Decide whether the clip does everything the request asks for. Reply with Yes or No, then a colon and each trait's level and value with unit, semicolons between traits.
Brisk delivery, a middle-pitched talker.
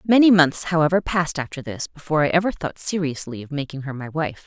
Yes: fast, 215 wpm; medium, 160 Hz